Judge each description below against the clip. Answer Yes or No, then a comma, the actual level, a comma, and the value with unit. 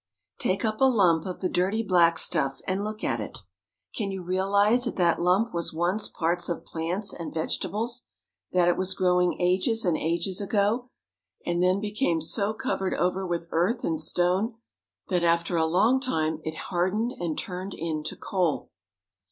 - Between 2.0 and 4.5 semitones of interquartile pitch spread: Yes, average, 3.3 semitones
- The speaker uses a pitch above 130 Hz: Yes, medium, 185 Hz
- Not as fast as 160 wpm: No, average, 175 wpm